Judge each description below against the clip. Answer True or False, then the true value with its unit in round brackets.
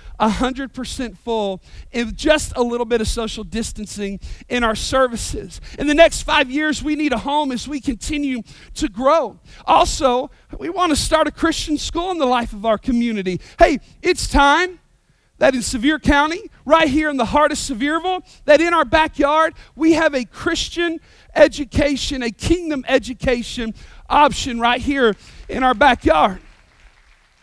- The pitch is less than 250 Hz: False (280 Hz)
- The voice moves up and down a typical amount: True (4.3 semitones)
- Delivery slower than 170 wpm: True (160 wpm)